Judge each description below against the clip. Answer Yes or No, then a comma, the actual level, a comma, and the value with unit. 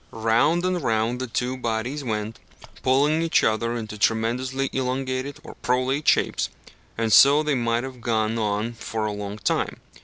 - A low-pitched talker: Yes, low, 120 Hz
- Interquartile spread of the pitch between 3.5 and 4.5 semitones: No, average, 3.1 semitones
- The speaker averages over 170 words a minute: No, average, 160 wpm